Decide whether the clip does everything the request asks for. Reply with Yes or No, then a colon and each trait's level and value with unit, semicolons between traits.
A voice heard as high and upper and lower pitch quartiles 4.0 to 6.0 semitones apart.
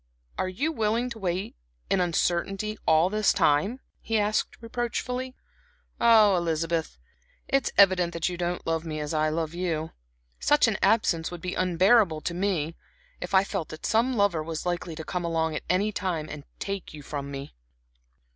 No: medium, 180 Hz; average, 4.5 semitones